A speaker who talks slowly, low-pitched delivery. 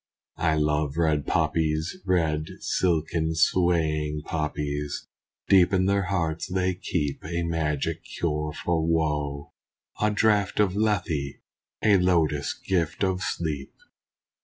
Yes: slow, 115 wpm; very low, 80 Hz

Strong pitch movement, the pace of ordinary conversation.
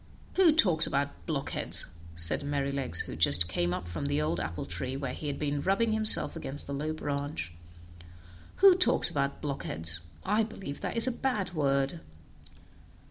Yes: wide, 6.3 semitones; average, 165 wpm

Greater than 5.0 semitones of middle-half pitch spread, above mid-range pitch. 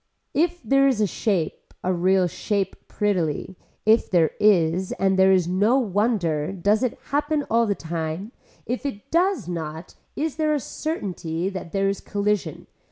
Yes: wide, 5.4 semitones; high, 200 Hz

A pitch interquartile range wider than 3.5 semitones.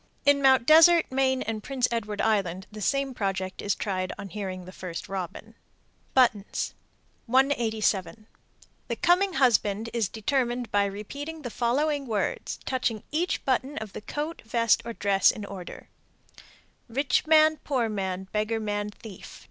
Yes: average, 4.9 semitones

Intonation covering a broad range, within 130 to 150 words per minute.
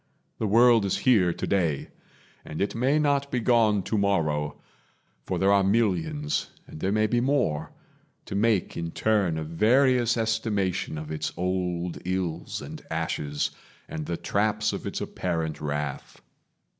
Yes: wide, 5.7 semitones; average, 145 wpm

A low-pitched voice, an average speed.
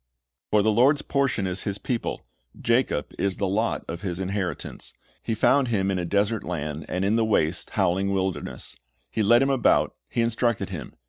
Yes: low, 100 Hz; average, 185 wpm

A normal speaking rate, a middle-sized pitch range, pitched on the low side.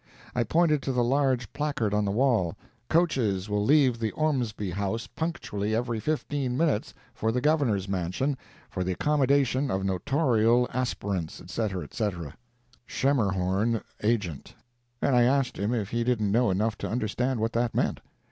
Yes: average, 145 wpm; average, 4.5 semitones; low, 120 Hz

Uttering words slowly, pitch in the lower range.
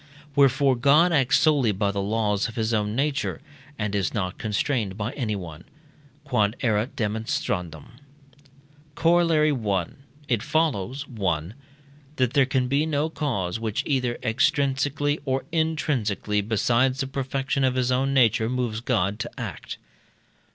Yes: slow, 130 wpm; low, 125 Hz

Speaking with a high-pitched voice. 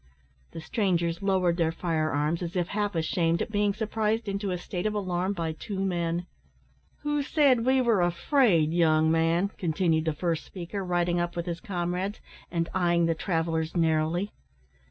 No: medium, 175 Hz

